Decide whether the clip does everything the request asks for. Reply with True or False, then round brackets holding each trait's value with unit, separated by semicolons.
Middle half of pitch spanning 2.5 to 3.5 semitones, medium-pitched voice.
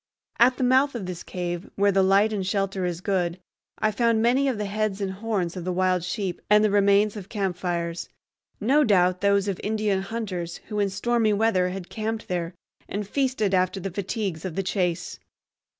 False (2.8 semitones; 200 Hz)